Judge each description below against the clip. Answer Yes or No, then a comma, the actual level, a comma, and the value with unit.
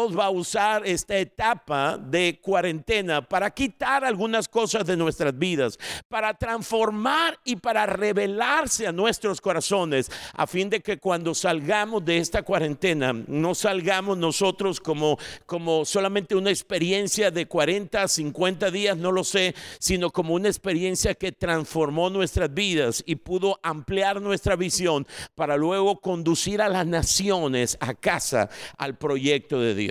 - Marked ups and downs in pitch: No, average, 3.6 semitones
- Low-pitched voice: No, medium, 185 Hz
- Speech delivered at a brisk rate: No, average, 140 wpm